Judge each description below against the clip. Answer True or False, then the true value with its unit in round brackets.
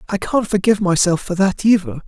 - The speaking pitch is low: False (190 Hz)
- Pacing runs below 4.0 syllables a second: False (5.9 syllables/s)